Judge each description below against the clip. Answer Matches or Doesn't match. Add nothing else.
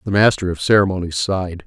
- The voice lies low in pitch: Matches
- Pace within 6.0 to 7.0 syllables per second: Matches